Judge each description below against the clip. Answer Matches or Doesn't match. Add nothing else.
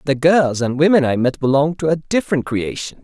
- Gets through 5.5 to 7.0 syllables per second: Matches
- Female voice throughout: Doesn't match